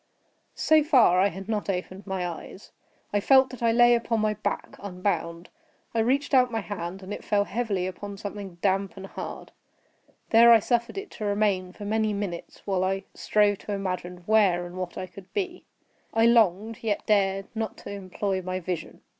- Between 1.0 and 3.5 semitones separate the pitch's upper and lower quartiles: Yes, average, 3.2 semitones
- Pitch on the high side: Yes, high, 200 Hz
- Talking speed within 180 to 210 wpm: Yes, average, 190 wpm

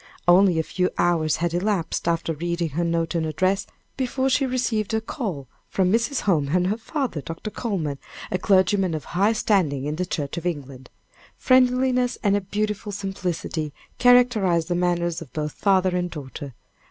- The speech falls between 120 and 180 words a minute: Yes, average, 170 wpm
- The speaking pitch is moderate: Yes, medium, 180 Hz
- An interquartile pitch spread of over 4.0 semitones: Yes, average, 4.6 semitones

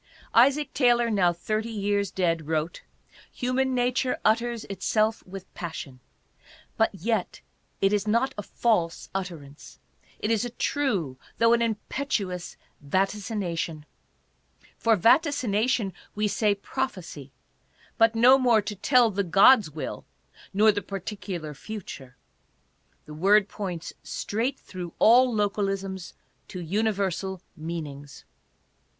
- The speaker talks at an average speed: No, slow, 120 wpm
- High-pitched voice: Yes, high, 205 Hz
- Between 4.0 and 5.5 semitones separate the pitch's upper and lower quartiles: Yes, average, 4.4 semitones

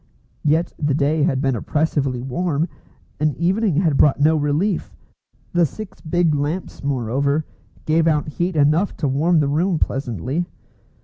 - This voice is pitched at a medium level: Yes, medium, 150 Hz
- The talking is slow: No, average, 145 wpm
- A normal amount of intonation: Yes, average, 3.2 semitones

